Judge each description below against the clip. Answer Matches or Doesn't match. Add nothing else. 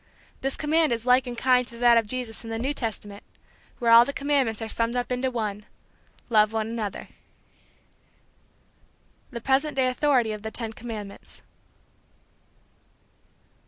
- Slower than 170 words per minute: Matches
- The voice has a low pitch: Doesn't match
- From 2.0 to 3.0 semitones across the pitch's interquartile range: Matches